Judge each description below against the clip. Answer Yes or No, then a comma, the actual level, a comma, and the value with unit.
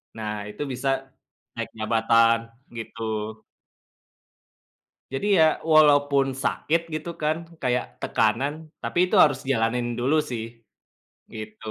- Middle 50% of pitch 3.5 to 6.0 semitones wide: Yes, average, 4.3 semitones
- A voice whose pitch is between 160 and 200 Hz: No, low, 120 Hz